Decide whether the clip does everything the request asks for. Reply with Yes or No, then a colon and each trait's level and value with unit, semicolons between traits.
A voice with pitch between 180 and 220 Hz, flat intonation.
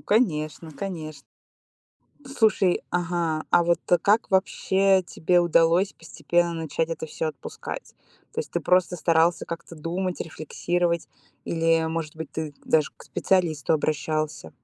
No: medium, 165 Hz; narrow, 2.1 semitones